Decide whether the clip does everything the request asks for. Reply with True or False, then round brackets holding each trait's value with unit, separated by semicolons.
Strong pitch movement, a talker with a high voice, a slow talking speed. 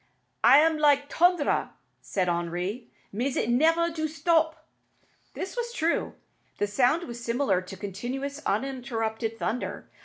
True (6.2 semitones; 260 Hz; 130 wpm)